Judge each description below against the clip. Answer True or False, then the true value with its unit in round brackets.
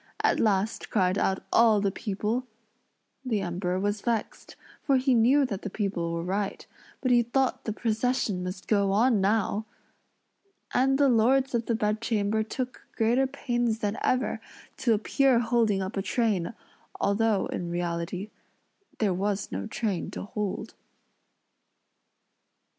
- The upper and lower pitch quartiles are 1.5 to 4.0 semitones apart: True (3.5 semitones)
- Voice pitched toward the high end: True (215 Hz)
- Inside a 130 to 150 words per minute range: True (140 wpm)